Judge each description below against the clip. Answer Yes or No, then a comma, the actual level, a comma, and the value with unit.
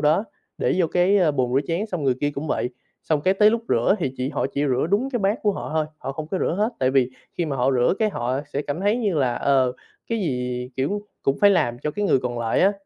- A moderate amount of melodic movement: No, wide, 7.1 semitones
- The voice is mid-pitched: Yes, medium, 150 Hz